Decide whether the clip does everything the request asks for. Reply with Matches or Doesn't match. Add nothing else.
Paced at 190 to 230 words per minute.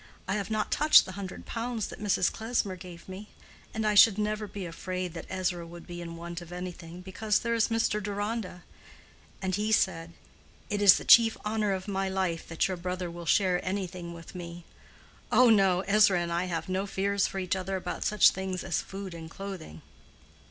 Matches